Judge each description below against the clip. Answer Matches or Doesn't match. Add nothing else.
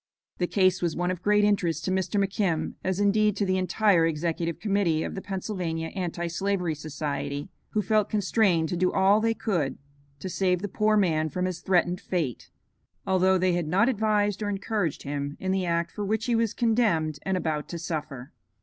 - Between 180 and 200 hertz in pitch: Matches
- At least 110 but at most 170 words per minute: Doesn't match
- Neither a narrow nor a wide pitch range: Matches